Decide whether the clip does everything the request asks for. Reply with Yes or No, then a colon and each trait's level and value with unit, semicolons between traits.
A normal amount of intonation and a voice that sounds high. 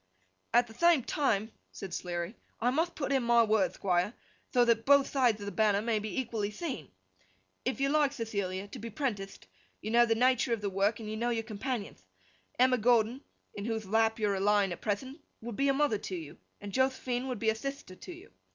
Yes: average, 4.1 semitones; high, 225 Hz